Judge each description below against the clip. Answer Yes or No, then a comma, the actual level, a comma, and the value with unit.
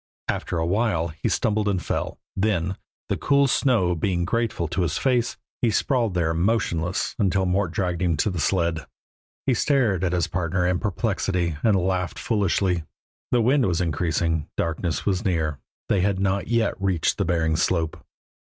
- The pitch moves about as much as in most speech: Yes, average, 3.8 semitones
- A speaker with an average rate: Yes, average, 170 wpm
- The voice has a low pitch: Yes, very low, 90 Hz